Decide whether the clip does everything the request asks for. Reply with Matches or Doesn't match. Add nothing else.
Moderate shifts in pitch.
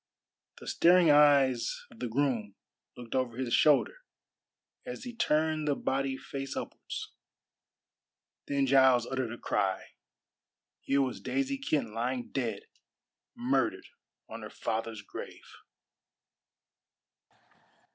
Matches